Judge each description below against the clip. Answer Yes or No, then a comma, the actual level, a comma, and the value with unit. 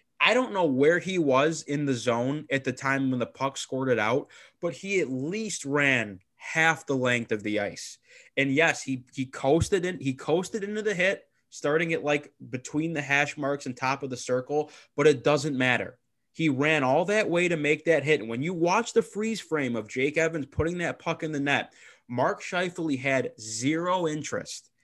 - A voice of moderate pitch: Yes, medium, 145 Hz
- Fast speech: Yes, fast, 210 wpm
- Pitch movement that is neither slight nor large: Yes, average, 3.9 semitones